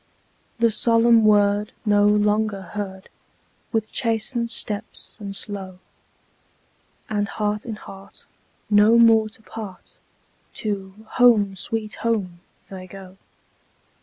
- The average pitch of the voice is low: No, high, 210 Hz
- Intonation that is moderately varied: No, narrow, 2.0 semitones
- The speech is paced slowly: Yes, slow, 105 wpm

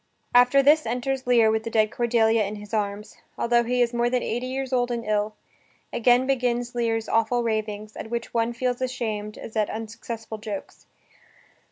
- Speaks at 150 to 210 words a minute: Yes, average, 180 wpm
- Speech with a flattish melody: Yes, narrow, 2.1 semitones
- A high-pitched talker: Yes, high, 235 Hz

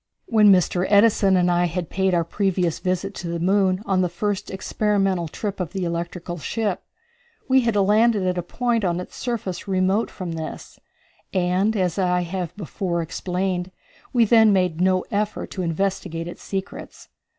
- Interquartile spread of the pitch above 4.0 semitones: No, narrow, 2.4 semitones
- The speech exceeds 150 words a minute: Yes, average, 170 wpm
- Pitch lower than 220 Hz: Yes, medium, 185 Hz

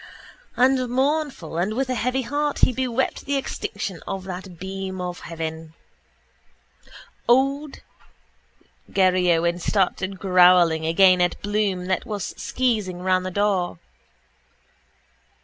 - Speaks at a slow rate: Yes, slow, 115 wpm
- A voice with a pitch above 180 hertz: Yes, high, 190 Hz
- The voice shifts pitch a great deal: Yes, wide, 5.8 semitones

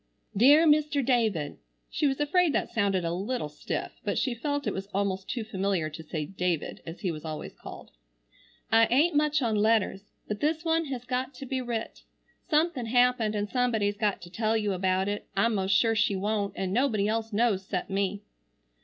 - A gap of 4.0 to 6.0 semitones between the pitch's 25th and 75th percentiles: Yes, average, 4.8 semitones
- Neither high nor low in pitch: No, high, 220 Hz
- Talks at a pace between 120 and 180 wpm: No, average, 195 wpm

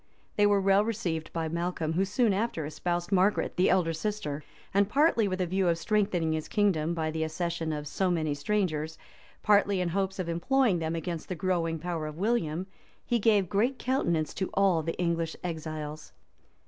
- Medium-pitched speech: Yes, medium, 175 Hz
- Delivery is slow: No, average, 185 wpm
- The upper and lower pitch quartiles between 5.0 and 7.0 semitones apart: No, average, 3.8 semitones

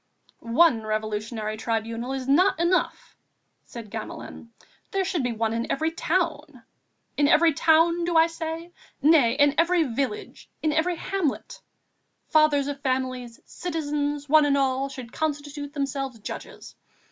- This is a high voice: Yes, very high, 285 Hz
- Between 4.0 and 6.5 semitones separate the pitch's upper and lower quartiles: Yes, average, 4.5 semitones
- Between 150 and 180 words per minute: No, slow, 135 wpm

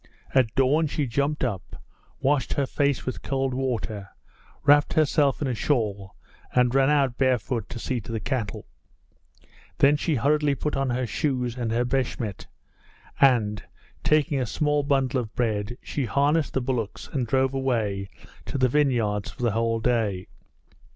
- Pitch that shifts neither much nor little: Yes, average, 3.5 semitones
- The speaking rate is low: No, average, 160 wpm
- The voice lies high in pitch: No, low, 130 Hz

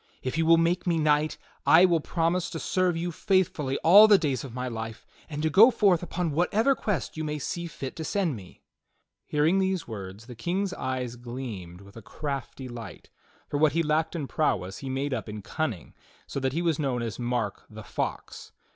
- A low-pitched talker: No, medium, 150 Hz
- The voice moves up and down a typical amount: No, wide, 5.7 semitones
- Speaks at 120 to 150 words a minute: No, fast, 205 wpm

